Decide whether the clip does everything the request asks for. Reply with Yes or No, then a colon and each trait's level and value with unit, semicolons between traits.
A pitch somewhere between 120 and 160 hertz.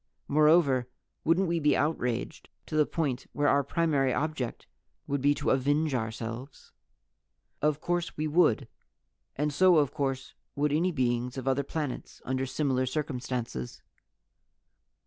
Yes: medium, 140 Hz